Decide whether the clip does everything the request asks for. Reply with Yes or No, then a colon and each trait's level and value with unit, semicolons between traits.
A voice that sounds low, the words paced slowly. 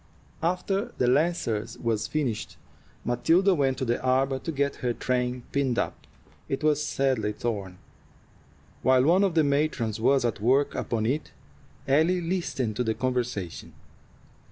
No: low, 130 Hz; average, 145 wpm